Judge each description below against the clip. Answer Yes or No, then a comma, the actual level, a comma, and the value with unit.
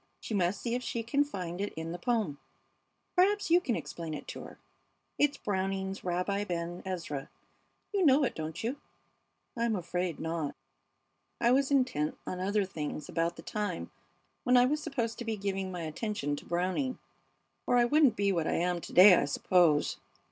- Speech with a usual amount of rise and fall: No, wide, 5.9 semitones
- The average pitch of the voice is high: Yes, high, 195 Hz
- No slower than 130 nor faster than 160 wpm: No, average, 185 wpm